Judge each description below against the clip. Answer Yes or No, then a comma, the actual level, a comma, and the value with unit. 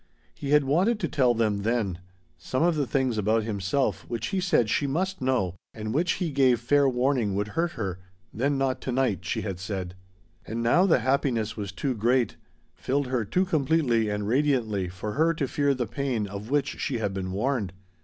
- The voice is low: Yes, low, 125 Hz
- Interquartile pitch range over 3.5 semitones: Yes, average, 5.0 semitones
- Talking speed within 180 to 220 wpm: Yes, average, 200 wpm